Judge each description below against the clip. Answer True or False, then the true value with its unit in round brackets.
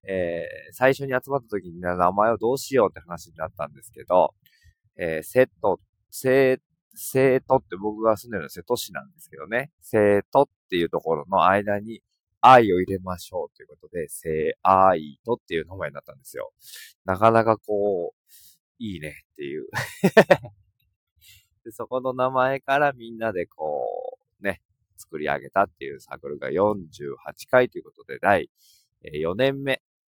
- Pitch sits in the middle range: False (125 Hz)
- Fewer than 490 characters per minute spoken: True (305 characters per minute)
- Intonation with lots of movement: True (6.3 semitones)